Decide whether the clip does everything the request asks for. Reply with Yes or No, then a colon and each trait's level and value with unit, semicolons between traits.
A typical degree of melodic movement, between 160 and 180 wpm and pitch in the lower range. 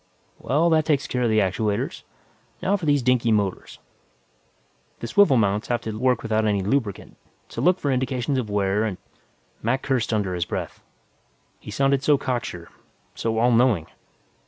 Yes: average, 4.2 semitones; average, 170 wpm; low, 120 Hz